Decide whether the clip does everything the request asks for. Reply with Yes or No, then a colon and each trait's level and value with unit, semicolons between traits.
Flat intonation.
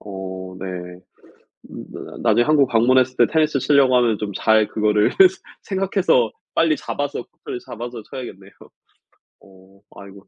No: average, 5.1 semitones